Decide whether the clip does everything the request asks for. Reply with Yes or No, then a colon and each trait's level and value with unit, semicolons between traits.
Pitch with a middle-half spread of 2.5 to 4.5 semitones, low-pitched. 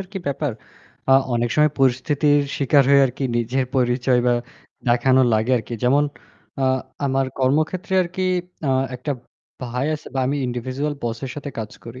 Yes: average, 2.9 semitones; low, 130 Hz